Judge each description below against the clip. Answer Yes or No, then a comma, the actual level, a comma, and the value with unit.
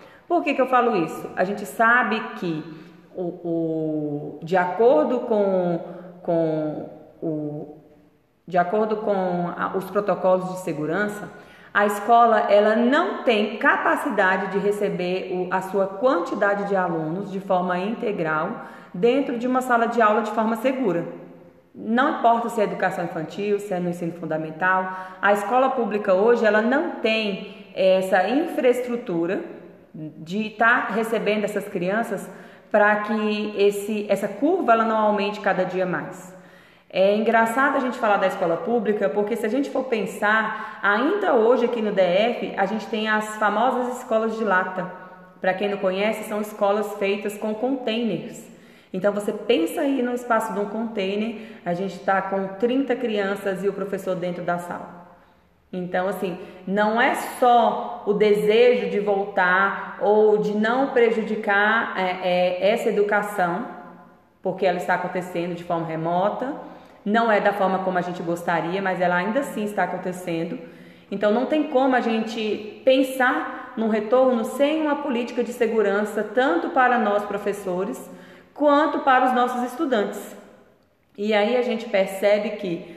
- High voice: Yes, high, 205 Hz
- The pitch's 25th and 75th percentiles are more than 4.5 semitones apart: No, average, 3.9 semitones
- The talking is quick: No, average, 155 wpm